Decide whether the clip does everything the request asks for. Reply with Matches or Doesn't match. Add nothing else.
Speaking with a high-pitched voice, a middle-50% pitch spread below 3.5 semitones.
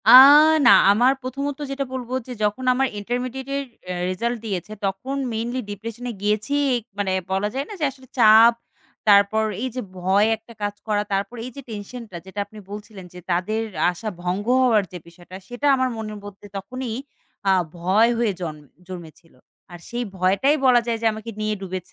Doesn't match